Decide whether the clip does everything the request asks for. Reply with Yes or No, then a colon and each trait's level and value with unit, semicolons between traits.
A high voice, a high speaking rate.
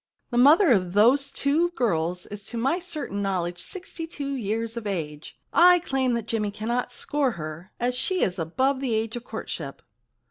No: high, 235 Hz; average, 180 wpm